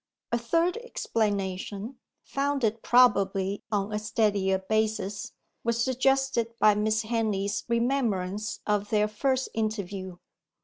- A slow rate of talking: Yes, slow, 105 wpm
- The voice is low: No, high, 215 Hz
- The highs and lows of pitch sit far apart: No, average, 2.8 semitones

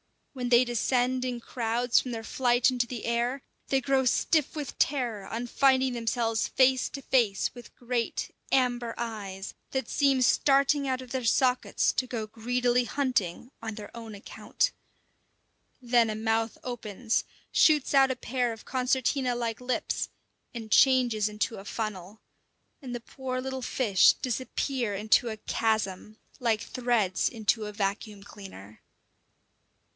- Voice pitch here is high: Yes, high, 240 Hz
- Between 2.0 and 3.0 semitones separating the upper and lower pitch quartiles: Yes, average, 2.7 semitones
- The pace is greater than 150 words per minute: No, average, 145 wpm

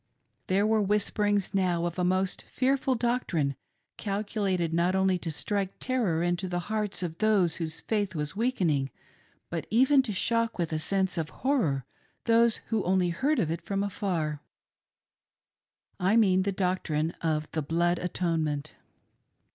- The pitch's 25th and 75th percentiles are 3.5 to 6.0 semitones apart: Yes, average, 4.1 semitones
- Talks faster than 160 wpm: No, average, 155 wpm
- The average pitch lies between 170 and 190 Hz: Yes, medium, 185 Hz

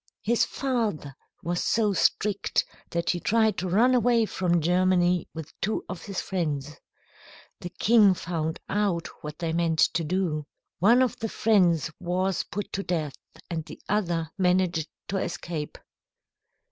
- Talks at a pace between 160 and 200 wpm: No, average, 145 wpm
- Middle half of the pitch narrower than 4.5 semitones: Yes, average, 3.7 semitones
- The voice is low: No, medium, 180 Hz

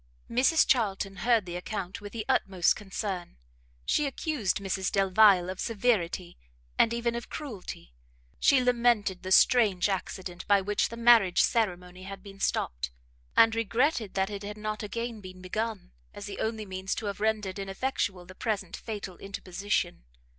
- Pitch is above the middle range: Yes, high, 205 Hz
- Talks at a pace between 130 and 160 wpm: Yes, average, 155 wpm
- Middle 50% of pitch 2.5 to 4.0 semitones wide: Yes, average, 3.4 semitones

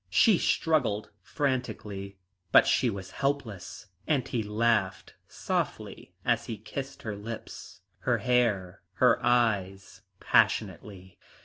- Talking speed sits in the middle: No, slow, 110 wpm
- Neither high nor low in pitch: No, low, 110 Hz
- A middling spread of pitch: Yes, average, 4.0 semitones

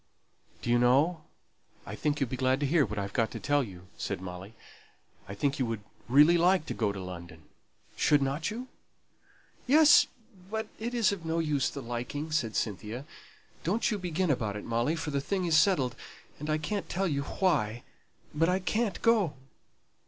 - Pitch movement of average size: No, wide, 7.1 semitones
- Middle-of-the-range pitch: Yes, medium, 145 Hz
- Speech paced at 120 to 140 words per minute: No, average, 180 wpm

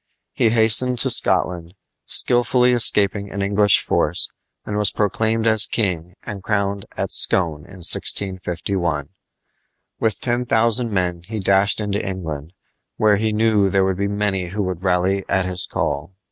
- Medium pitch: No, low, 100 Hz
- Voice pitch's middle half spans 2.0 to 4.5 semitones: Yes, average, 3.0 semitones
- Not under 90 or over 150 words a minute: Yes, average, 145 wpm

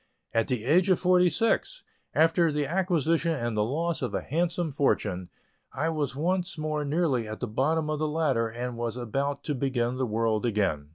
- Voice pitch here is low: No, medium, 145 Hz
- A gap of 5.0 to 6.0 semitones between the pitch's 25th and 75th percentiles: Yes, wide, 5.6 semitones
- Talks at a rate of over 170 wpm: Yes, average, 190 wpm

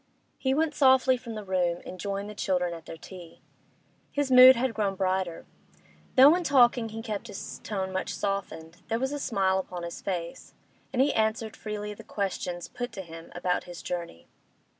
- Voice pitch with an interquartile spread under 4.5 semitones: No, wide, 5.4 semitones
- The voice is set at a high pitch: Yes, high, 200 Hz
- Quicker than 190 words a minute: No, average, 185 wpm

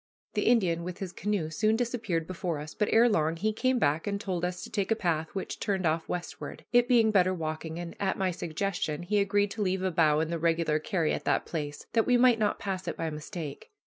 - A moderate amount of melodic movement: Yes, average, 4.4 semitones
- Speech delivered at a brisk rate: Yes, fast, 235 wpm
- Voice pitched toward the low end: No, medium, 180 Hz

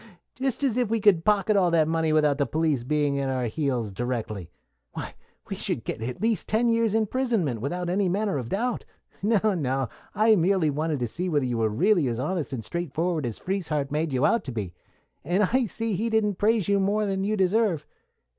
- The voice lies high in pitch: No, medium, 175 Hz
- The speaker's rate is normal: No, fast, 210 wpm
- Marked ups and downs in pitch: Yes, wide, 7.2 semitones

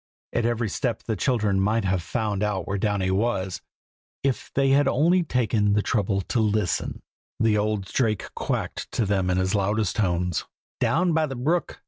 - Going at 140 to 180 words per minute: Yes, average, 175 wpm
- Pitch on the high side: No, low, 105 Hz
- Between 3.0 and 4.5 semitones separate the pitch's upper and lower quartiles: Yes, average, 3.9 semitones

